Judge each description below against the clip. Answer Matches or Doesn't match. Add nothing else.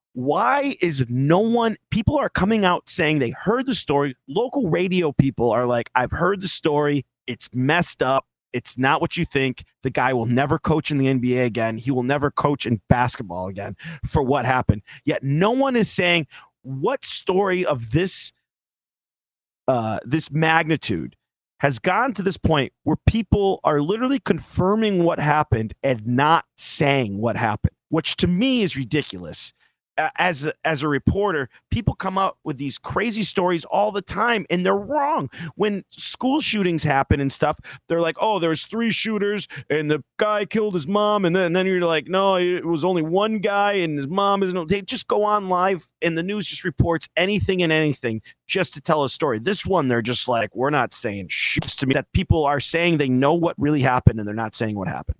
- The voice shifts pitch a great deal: Matches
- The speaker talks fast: Doesn't match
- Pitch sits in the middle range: Matches